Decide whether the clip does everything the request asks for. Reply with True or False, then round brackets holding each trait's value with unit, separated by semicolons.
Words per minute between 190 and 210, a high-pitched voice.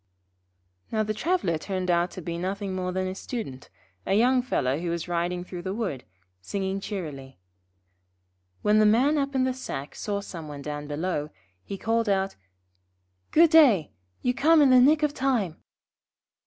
False (170 wpm; 195 Hz)